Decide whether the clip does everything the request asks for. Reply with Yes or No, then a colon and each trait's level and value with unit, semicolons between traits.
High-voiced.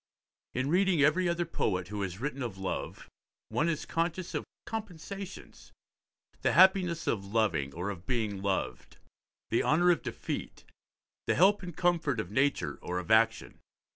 No: medium, 140 Hz